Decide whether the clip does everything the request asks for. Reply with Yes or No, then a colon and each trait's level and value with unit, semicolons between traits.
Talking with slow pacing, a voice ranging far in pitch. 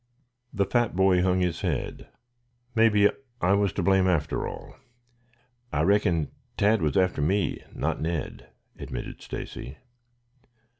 No: slow, 130 wpm; average, 3.1 semitones